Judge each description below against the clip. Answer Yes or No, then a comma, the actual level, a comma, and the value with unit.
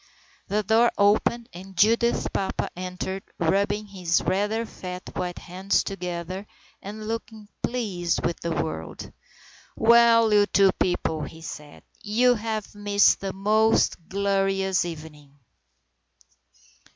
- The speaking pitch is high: Yes, high, 195 Hz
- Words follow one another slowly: Yes, slow, 115 wpm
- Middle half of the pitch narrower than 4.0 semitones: Yes, average, 3.3 semitones